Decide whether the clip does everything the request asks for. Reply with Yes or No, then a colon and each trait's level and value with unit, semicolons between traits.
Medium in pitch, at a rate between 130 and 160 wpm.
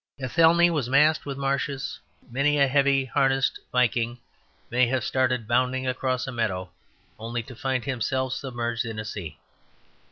No: low, 130 Hz; average, 150 wpm